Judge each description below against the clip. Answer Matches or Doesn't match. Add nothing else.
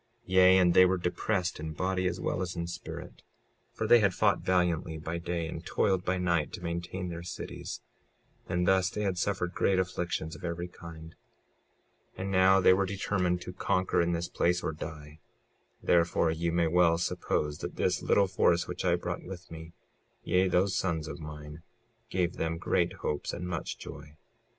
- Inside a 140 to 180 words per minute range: Doesn't match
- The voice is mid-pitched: Doesn't match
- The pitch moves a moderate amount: Doesn't match